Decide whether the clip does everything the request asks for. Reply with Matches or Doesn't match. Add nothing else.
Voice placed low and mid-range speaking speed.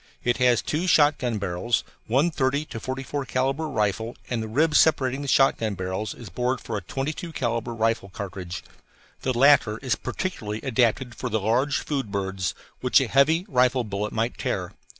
Matches